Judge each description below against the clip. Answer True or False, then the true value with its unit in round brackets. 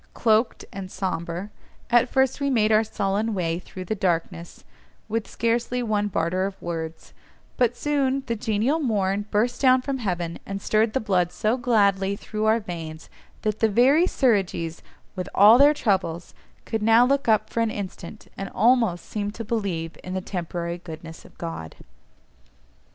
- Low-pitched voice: False (210 Hz)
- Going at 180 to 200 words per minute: False (165 wpm)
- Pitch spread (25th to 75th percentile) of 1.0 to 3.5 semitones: False (4.3 semitones)